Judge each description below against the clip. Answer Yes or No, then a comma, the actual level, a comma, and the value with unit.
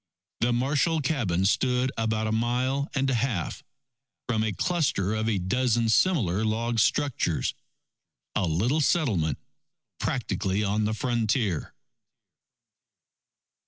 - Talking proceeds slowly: Yes, slow, 115 wpm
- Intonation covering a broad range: No, average, 3.7 semitones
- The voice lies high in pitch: No, low, 115 Hz